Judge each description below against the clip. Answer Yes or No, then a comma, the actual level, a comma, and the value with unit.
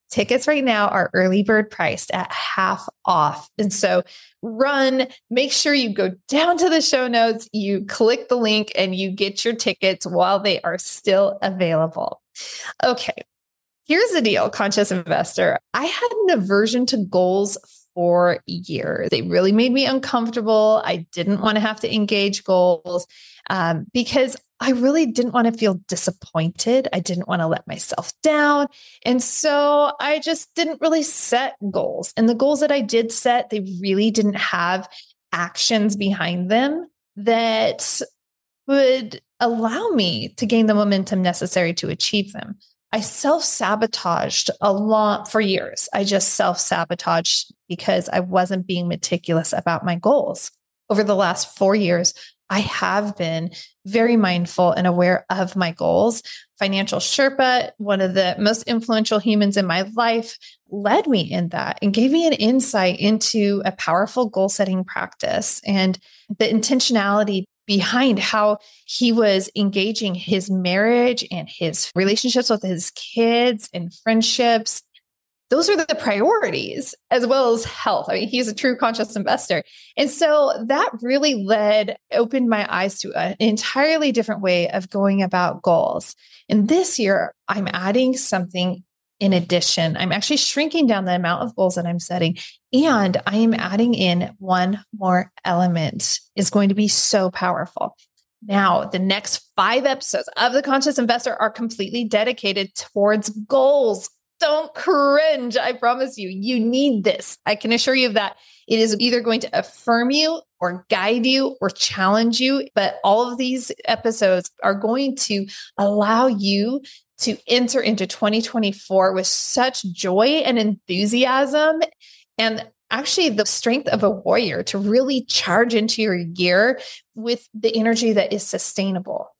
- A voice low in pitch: No, high, 215 Hz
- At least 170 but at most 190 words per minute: No, average, 155 wpm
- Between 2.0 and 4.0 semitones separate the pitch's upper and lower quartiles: No, average, 4.6 semitones